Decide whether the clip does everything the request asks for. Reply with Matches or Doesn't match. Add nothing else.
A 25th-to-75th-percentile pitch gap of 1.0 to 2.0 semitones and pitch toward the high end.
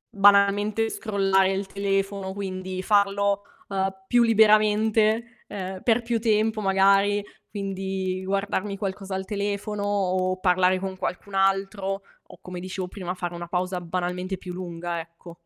Matches